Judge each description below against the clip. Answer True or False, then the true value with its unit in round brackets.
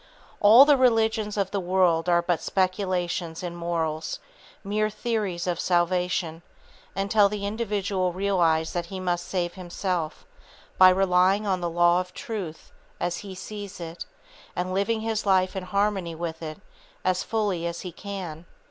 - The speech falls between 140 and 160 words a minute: True (155 wpm)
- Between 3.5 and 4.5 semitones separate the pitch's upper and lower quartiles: False (2.7 semitones)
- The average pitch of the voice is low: False (185 Hz)